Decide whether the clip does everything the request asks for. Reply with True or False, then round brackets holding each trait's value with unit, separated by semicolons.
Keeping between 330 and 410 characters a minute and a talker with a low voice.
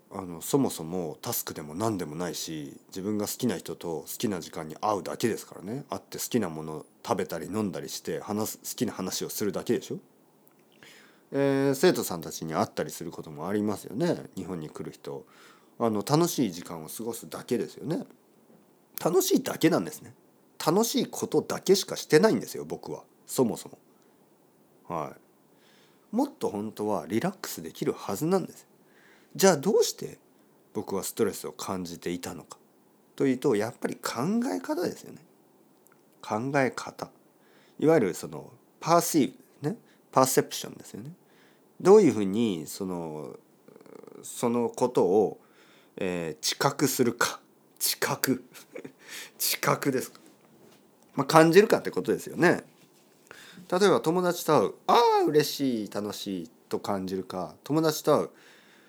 False (310 characters per minute; 125 Hz)